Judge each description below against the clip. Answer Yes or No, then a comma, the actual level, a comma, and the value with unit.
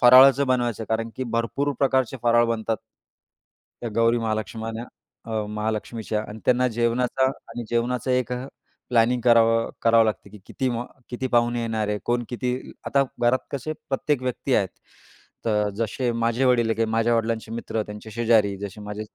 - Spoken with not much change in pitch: Yes, narrow, 2.0 semitones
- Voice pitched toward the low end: Yes, low, 115 Hz